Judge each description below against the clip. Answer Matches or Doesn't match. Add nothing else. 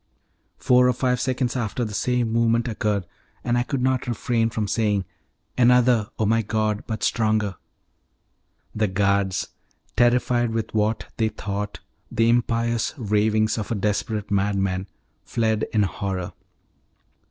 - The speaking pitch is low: Matches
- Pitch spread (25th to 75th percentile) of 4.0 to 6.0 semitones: Doesn't match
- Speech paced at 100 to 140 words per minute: Matches